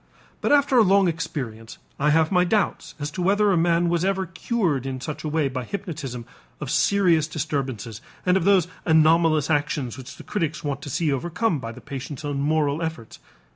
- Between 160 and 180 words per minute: No, average, 195 wpm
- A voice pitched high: No, medium, 160 Hz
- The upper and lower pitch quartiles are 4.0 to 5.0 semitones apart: Yes, average, 4.3 semitones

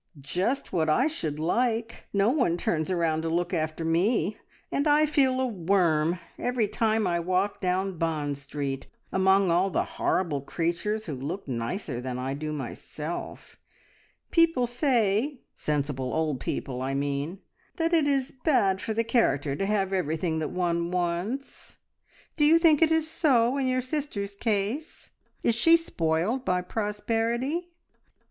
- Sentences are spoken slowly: No, average, 155 wpm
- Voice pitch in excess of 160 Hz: Yes, high, 190 Hz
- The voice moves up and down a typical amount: No, wide, 7.5 semitones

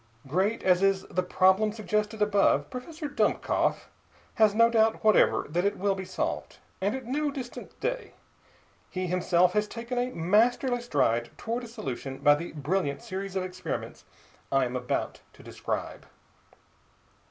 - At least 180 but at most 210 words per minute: No, average, 155 wpm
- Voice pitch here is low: No, high, 200 Hz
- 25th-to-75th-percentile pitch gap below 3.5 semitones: No, average, 4.3 semitones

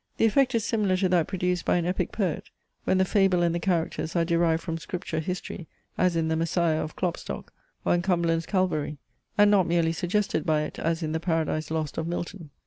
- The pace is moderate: No, fast, 215 wpm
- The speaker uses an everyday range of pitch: No, narrow, 2.3 semitones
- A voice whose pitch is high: No, medium, 170 Hz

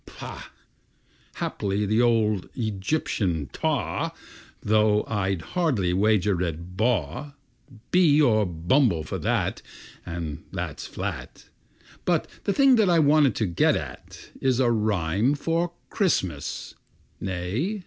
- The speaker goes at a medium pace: No, slow, 120 wpm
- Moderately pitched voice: No, low, 110 Hz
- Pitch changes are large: Yes, wide, 7.8 semitones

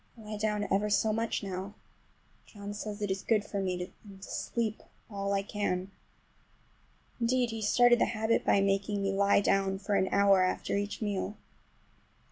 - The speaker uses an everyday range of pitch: No, narrow, 1.6 semitones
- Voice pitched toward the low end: No, high, 205 Hz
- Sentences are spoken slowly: No, average, 175 wpm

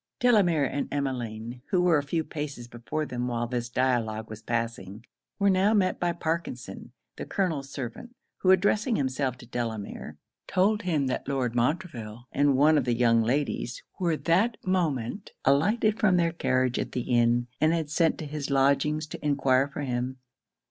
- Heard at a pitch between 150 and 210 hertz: No, medium, 140 Hz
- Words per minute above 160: Yes, average, 170 wpm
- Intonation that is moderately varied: No, wide, 5.7 semitones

